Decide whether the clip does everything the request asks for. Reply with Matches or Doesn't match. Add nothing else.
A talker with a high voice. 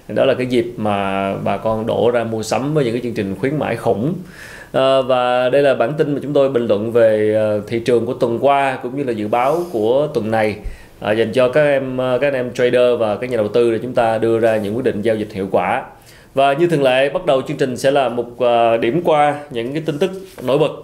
Doesn't match